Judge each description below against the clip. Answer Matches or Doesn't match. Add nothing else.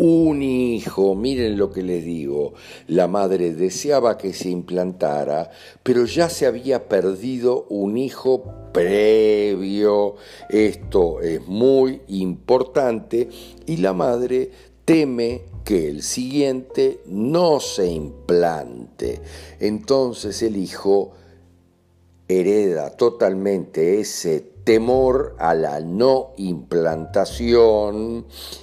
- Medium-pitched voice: Doesn't match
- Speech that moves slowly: Matches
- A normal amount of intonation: Doesn't match